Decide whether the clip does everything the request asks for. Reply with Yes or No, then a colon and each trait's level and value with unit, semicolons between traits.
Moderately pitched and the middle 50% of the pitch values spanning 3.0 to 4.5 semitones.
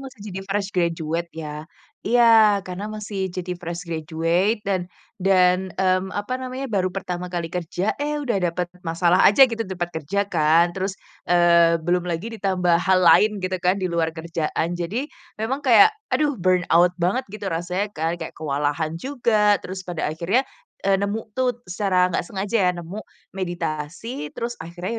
Yes: medium, 180 Hz; average, 3.3 semitones